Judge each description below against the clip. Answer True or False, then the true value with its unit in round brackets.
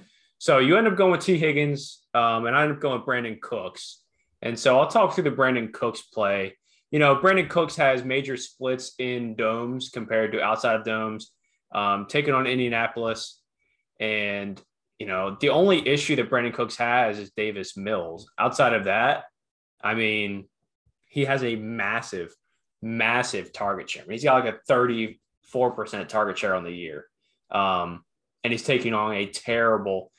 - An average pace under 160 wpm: False (175 wpm)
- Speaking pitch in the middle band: False (115 Hz)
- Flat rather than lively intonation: False (3.6 semitones)